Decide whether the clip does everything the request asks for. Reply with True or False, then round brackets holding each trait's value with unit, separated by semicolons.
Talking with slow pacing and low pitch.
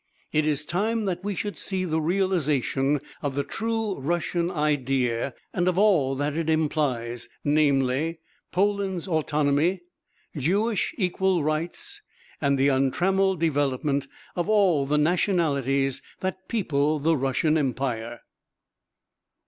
False (120 wpm; 155 Hz)